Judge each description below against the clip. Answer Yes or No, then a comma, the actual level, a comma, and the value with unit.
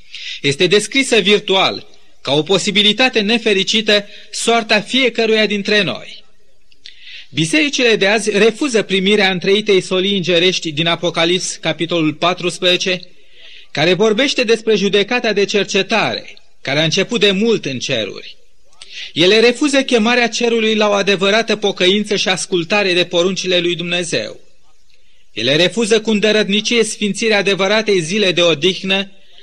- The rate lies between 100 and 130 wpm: Yes, average, 120 wpm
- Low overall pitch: No, high, 200 Hz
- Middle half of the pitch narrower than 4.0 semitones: Yes, average, 3.4 semitones